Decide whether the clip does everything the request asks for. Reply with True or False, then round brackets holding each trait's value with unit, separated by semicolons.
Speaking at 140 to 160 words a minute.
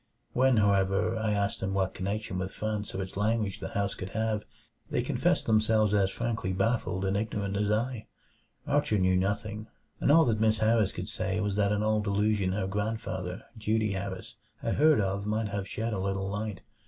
False (190 wpm)